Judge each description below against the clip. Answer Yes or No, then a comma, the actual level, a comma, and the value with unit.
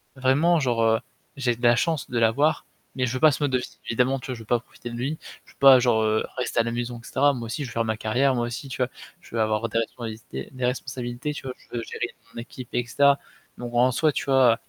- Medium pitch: No, low, 125 Hz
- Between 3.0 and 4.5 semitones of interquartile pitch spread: No, narrow, 2.4 semitones